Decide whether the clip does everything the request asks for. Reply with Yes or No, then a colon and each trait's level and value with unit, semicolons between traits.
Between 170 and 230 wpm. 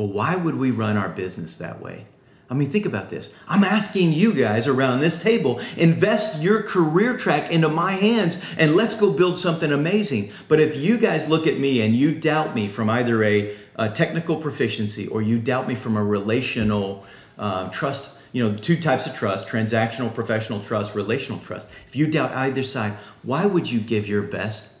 Yes: average, 200 wpm